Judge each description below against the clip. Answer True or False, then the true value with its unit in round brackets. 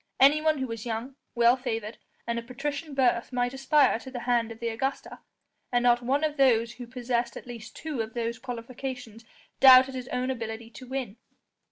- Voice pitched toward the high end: True (245 Hz)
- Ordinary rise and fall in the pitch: False (2.2 semitones)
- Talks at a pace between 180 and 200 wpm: True (190 wpm)